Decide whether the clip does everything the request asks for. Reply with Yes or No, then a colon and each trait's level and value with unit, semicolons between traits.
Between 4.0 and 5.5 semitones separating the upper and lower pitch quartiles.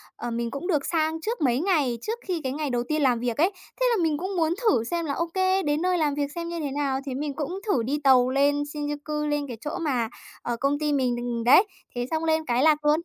No: average, 3.5 semitones